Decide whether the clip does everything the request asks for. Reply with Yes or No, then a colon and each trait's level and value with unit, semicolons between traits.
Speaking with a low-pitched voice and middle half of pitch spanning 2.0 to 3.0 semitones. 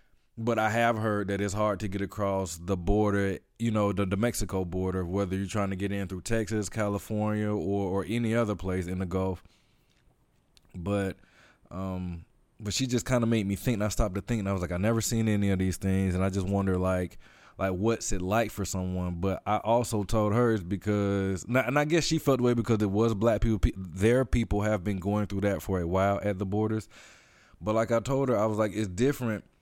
Yes: low, 105 Hz; average, 2.7 semitones